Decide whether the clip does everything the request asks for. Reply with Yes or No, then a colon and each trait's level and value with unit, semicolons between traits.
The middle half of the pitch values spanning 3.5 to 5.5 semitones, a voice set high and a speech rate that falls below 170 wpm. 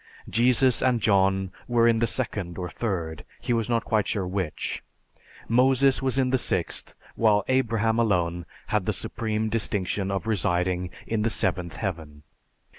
No: average, 4.2 semitones; low, 110 Hz; average, 155 wpm